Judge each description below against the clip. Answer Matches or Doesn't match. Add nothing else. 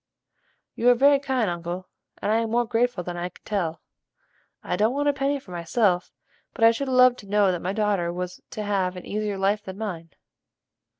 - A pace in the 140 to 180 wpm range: Doesn't match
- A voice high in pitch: Matches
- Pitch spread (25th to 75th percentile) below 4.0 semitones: Doesn't match